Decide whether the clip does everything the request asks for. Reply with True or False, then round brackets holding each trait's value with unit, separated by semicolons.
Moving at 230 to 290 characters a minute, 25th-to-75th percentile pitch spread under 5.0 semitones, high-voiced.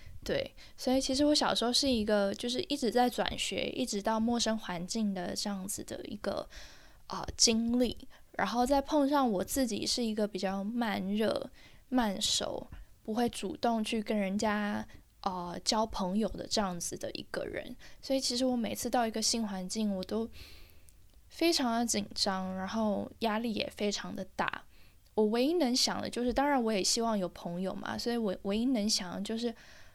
True (265 characters per minute; 3.5 semitones; 225 Hz)